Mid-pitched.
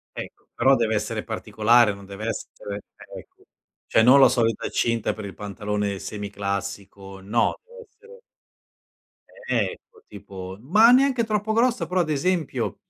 No: low, 115 Hz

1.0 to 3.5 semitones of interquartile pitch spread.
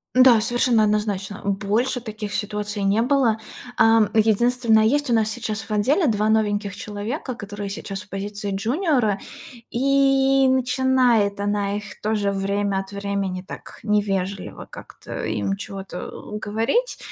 Yes: average, 3.1 semitones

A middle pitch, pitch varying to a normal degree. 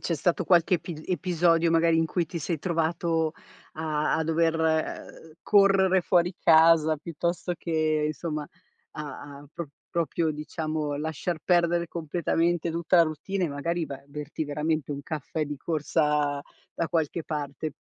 No: medium, 160 Hz; narrow, 2.0 semitones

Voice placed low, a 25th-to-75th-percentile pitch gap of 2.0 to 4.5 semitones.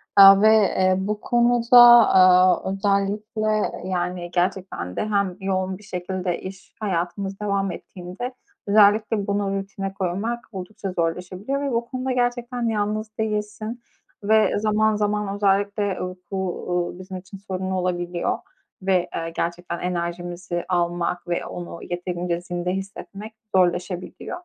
No: high, 195 Hz; average, 2.9 semitones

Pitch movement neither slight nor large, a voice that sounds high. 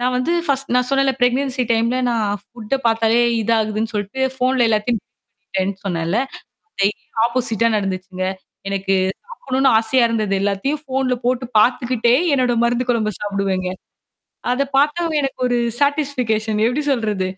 Yes: average, 3.7 semitones; high, 235 Hz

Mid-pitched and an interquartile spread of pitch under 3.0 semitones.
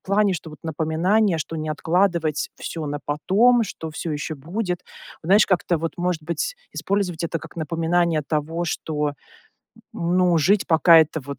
Yes: medium, 165 Hz; narrow, 2.6 semitones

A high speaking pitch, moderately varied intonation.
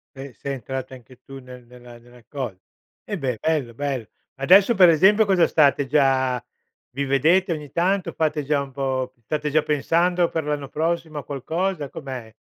No: medium, 140 Hz; average, 3.9 semitones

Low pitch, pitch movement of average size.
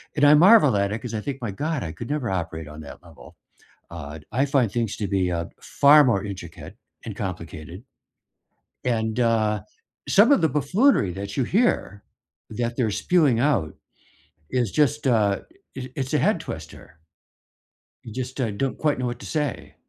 No: low, 115 Hz; wide, 6.3 semitones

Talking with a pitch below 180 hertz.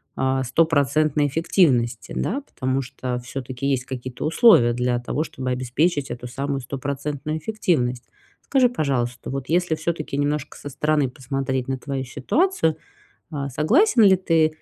Yes: medium, 140 Hz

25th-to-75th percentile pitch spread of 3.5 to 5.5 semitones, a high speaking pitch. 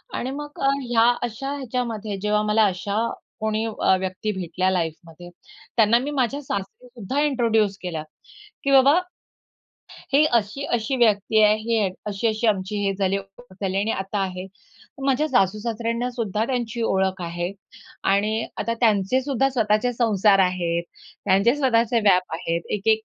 Yes: average, 3.9 semitones; high, 215 Hz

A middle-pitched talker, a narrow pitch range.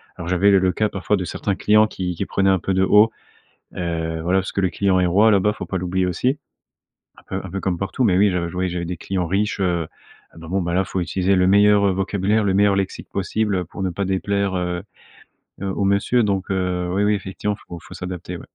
No: very low, 95 Hz; narrow, 1.9 semitones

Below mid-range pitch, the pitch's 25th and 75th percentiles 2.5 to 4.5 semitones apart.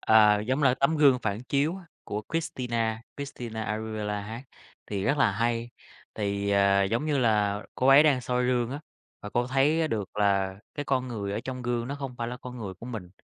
Yes: low, 120 Hz; average, 4.0 semitones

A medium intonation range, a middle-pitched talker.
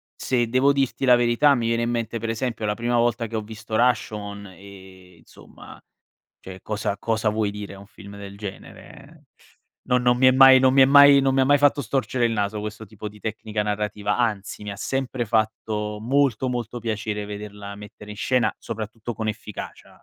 No: average, 3.0 semitones; low, 110 Hz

